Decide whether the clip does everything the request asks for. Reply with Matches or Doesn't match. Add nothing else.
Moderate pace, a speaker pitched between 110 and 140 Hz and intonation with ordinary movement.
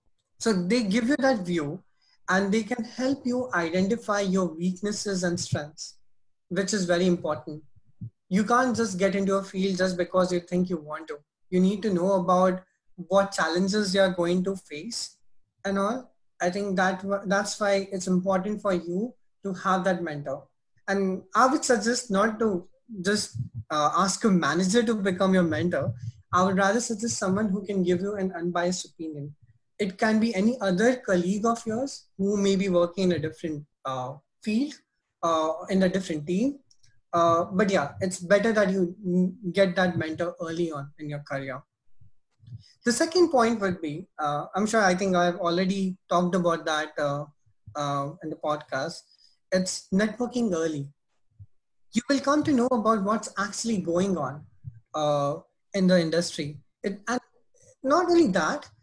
Doesn't match